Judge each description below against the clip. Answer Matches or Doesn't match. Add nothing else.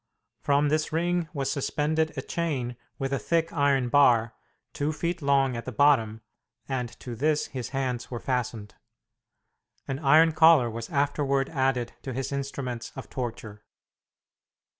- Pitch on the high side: Doesn't match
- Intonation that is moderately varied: Matches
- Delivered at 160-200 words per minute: Doesn't match